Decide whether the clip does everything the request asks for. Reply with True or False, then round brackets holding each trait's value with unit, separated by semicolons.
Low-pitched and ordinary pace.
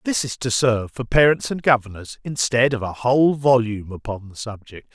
True (120 Hz; 195 wpm)